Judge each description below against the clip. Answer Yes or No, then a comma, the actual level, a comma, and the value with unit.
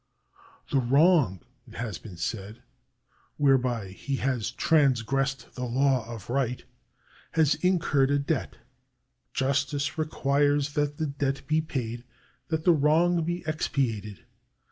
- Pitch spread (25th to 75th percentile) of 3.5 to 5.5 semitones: Yes, average, 3.8 semitones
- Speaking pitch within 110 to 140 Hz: Yes, low, 135 Hz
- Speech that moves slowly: Yes, slow, 130 wpm